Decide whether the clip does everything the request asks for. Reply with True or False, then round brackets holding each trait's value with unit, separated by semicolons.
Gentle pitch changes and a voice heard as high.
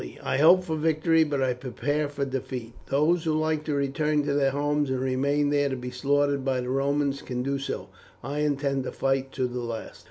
False (2.0 semitones; 140 Hz)